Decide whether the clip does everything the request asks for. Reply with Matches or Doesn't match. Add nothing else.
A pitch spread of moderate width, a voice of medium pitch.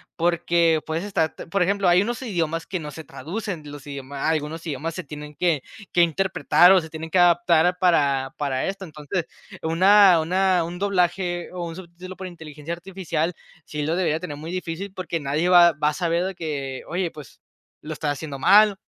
Matches